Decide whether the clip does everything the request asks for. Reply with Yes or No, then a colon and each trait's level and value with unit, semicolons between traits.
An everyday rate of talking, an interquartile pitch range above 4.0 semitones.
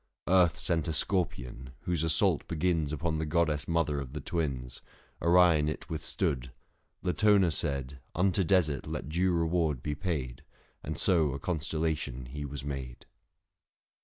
No: average, 150 wpm; average, 3.7 semitones